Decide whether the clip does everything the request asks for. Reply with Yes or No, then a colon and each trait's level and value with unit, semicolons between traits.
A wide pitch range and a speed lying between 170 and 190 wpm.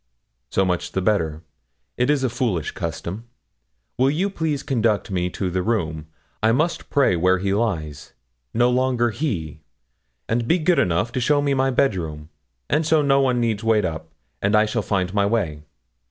Yes: wide, 6.4 semitones; average, 180 wpm